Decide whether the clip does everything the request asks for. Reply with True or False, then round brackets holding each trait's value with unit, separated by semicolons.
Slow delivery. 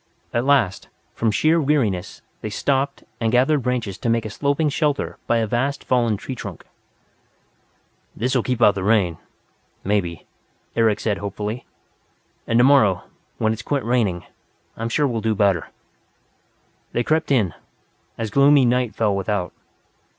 False (155 wpm)